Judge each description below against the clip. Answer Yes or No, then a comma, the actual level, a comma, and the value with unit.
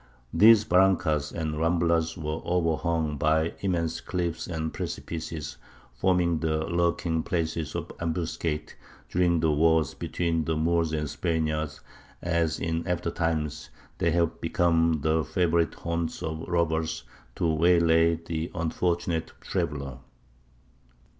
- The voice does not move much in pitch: Yes, narrow, 1.4 semitones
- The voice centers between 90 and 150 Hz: No, very low, 80 Hz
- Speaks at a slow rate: Yes, slow, 120 wpm